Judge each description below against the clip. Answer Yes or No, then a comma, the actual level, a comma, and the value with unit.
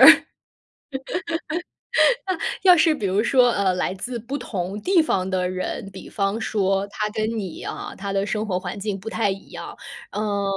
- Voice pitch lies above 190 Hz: Yes, high, 200 Hz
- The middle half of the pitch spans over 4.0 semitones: No, narrow, 2.5 semitones